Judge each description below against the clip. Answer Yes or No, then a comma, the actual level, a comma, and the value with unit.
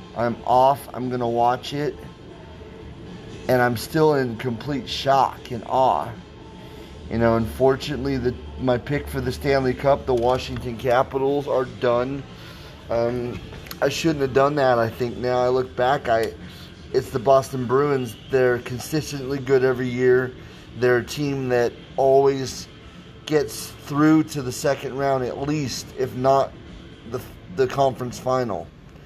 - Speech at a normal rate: Yes, average, 145 wpm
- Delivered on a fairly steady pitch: Yes, narrow, 2.0 semitones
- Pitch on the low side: Yes, low, 130 Hz